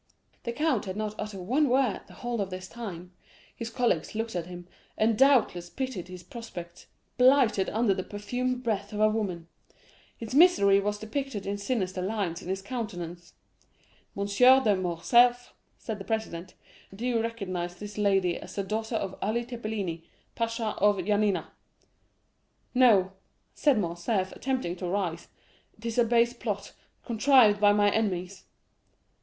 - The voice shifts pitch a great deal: No, average, 4.1 semitones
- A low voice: No, high, 210 Hz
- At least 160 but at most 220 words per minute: No, average, 150 wpm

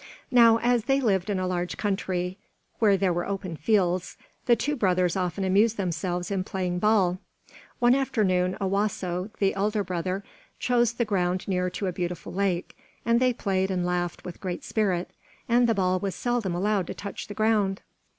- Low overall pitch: No, high, 195 Hz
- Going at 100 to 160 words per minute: No, average, 180 wpm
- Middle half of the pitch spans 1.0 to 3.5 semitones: Yes, average, 3.0 semitones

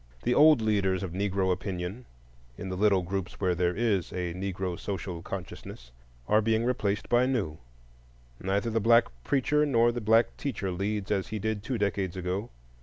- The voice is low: Yes, low, 100 Hz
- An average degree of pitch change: Yes, average, 3.4 semitones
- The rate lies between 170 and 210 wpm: Yes, average, 175 wpm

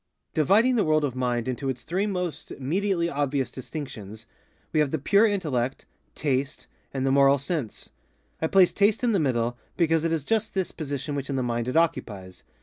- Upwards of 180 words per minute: Yes, average, 190 wpm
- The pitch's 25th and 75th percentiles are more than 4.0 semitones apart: Yes, average, 5.3 semitones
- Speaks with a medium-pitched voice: Yes, medium, 145 Hz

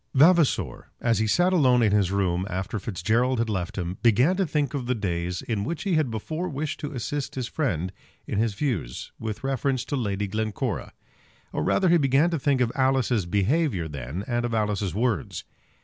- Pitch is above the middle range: No, low, 115 Hz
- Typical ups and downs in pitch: No, wide, 5.8 semitones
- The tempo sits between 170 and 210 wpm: Yes, average, 195 wpm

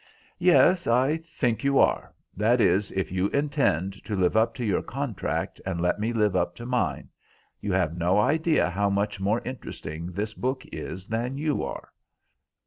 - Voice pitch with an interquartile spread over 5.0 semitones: Yes, wide, 5.4 semitones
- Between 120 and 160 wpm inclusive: No, average, 175 wpm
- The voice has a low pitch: Yes, low, 105 Hz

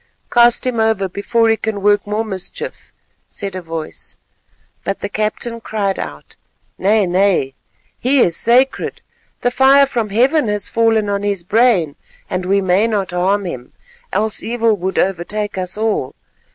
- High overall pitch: Yes, high, 205 Hz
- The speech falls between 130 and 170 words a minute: Yes, average, 155 wpm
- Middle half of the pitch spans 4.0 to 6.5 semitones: No, average, 3.2 semitones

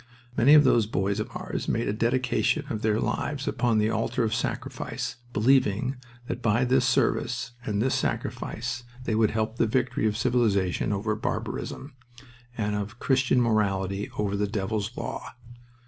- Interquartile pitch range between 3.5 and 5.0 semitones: No, average, 3.0 semitones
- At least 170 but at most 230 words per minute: No, average, 160 wpm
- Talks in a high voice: No, low, 110 Hz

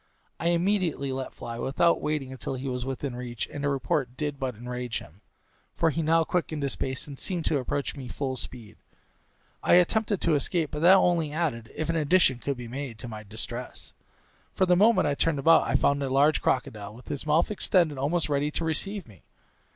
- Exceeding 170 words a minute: Yes, fast, 205 wpm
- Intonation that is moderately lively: Yes, average, 4.6 semitones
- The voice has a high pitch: No, medium, 140 Hz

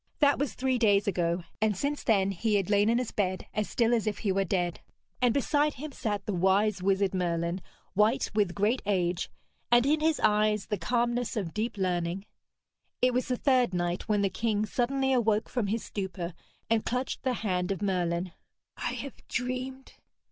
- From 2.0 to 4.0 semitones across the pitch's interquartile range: No, average, 4.4 semitones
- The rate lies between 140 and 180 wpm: No, average, 190 wpm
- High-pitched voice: Yes, high, 210 Hz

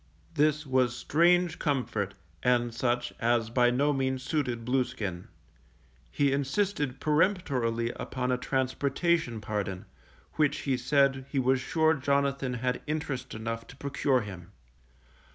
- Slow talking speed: Yes, slow, 125 wpm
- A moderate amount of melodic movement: Yes, average, 3.1 semitones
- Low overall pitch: Yes, low, 130 Hz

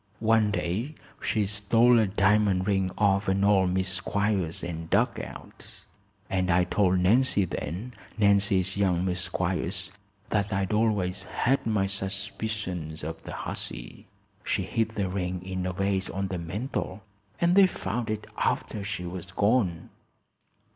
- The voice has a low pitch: Yes, very low, 95 Hz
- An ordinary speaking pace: Yes, average, 145 wpm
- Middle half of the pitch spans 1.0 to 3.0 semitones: Yes, narrow, 2.6 semitones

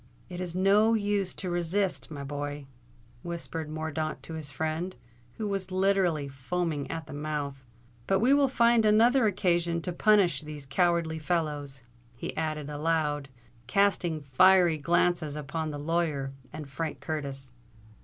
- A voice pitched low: No, medium, 165 Hz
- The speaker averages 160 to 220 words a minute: No, average, 145 wpm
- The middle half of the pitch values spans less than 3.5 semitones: No, average, 4.0 semitones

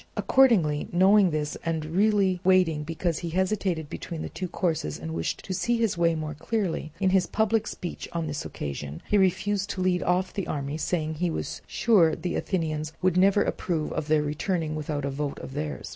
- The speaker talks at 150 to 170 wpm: No, average, 195 wpm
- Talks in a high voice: No, medium, 170 Hz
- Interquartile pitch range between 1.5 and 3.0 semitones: No, average, 3.6 semitones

